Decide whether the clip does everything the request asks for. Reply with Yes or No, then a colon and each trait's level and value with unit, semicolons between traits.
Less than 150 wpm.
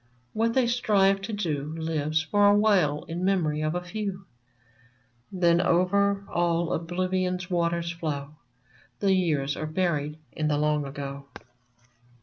Yes: average, 140 wpm